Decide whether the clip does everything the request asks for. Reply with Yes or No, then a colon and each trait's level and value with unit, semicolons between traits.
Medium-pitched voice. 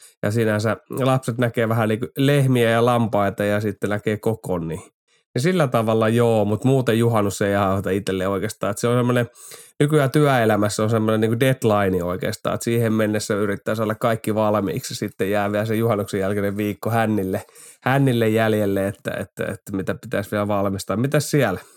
No: low, 110 Hz